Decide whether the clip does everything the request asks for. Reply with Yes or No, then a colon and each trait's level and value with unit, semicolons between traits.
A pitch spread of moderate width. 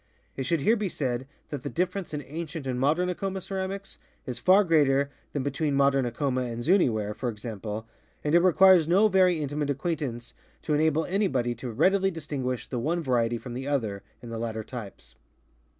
No: wide, 6.0 semitones